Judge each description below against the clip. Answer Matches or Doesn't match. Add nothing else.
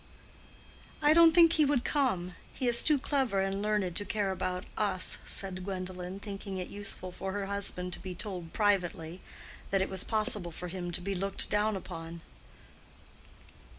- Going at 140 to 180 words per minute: Matches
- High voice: Matches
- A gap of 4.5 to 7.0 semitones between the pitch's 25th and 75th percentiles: Doesn't match